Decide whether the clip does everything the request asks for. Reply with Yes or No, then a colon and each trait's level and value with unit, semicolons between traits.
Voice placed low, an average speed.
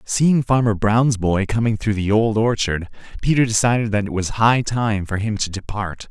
Yes: low, 110 Hz; average, 195 wpm